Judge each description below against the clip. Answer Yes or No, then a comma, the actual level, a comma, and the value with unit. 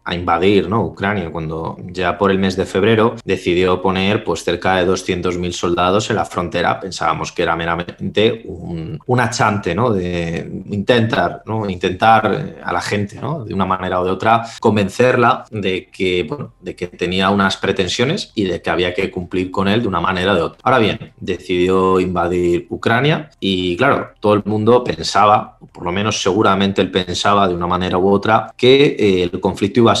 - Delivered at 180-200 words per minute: Yes, average, 185 wpm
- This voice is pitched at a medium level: No, very low, 95 Hz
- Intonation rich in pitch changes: No, average, 2.9 semitones